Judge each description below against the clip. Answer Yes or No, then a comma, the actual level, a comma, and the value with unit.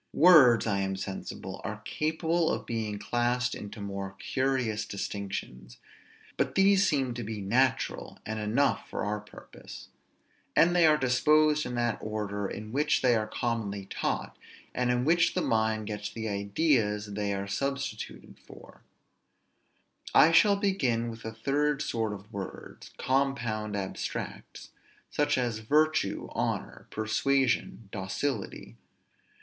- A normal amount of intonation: Yes, average, 4.9 semitones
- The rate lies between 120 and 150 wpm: Yes, slow, 135 wpm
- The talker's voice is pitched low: Yes, low, 115 Hz